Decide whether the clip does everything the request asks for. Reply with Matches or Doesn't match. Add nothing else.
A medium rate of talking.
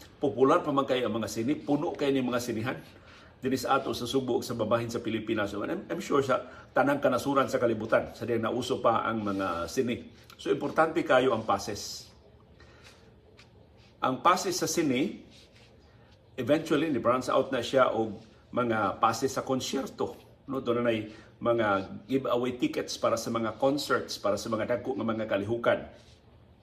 Doesn't match